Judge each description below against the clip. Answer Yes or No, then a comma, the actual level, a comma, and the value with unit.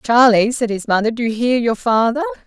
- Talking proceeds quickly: Yes, fast, 220 wpm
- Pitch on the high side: Yes, high, 230 Hz